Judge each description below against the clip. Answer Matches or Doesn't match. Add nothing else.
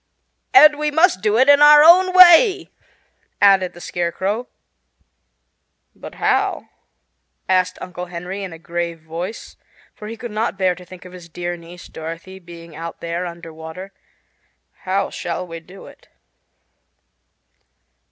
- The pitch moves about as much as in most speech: Matches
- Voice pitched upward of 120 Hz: Matches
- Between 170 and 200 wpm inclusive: Doesn't match